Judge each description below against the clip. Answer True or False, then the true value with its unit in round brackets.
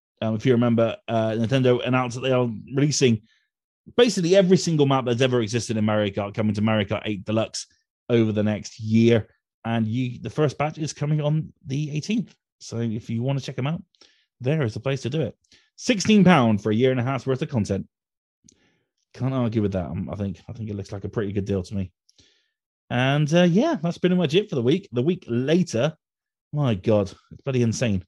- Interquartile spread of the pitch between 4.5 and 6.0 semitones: True (5.3 semitones)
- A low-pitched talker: True (120 Hz)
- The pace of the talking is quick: True (225 wpm)